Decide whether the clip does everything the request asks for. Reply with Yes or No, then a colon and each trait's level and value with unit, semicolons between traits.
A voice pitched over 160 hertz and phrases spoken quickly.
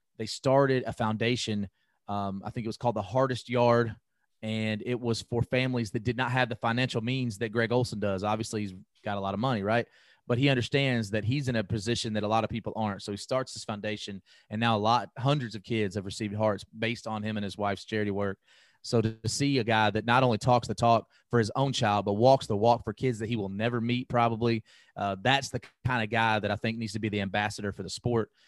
No: low, 115 Hz; fast, 250 wpm